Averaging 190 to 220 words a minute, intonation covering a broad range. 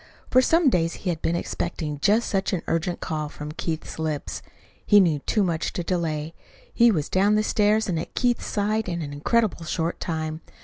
No: average, 195 wpm; average, 4.7 semitones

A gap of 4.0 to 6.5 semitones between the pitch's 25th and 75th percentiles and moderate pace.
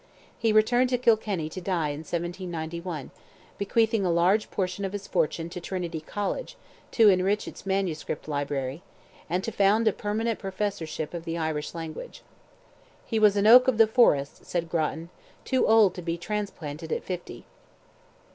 Yes: average, 4.4 semitones; average, 160 wpm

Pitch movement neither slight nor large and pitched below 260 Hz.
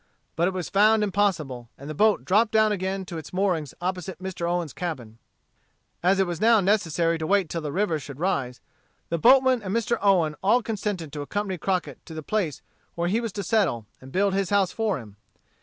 Yes: average, 4.2 semitones; medium, 185 Hz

